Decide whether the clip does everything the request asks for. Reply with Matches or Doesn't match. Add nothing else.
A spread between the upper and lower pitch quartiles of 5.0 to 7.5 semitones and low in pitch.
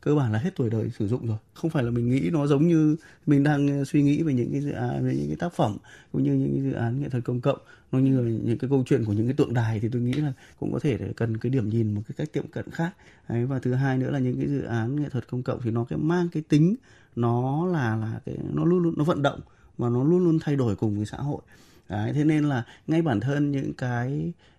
Doesn't match